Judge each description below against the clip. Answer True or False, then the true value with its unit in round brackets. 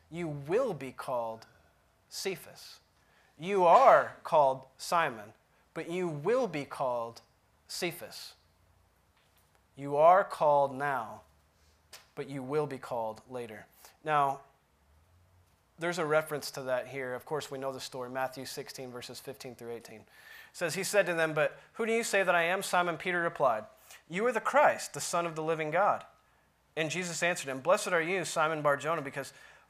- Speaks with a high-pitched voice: False (140 Hz)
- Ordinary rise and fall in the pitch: False (6.6 semitones)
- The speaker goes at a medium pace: True (165 wpm)